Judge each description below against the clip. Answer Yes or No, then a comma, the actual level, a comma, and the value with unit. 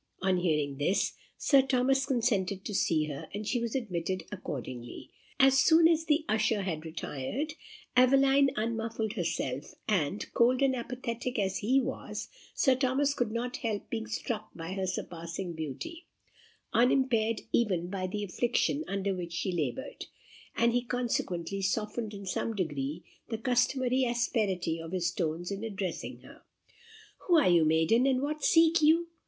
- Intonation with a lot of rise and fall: Yes, wide, 6.2 semitones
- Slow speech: No, average, 155 wpm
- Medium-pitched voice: No, high, 220 Hz